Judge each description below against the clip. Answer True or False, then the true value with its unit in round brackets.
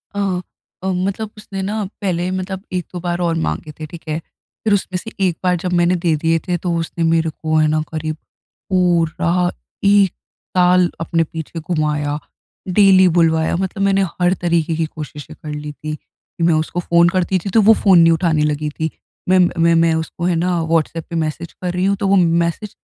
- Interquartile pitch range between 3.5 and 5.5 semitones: False (2.4 semitones)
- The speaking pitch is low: False (170 Hz)